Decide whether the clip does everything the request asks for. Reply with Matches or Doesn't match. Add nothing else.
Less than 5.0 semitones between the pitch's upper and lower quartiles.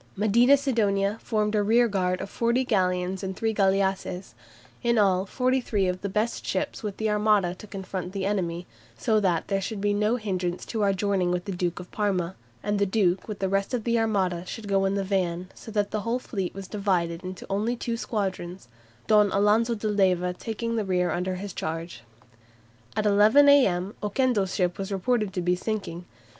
Matches